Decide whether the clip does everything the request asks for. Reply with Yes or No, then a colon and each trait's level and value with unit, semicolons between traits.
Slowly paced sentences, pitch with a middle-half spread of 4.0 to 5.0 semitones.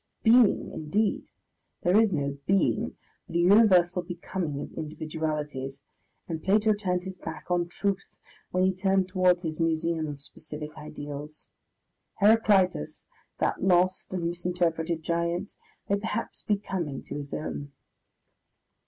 No: slow, 130 wpm; average, 3.6 semitones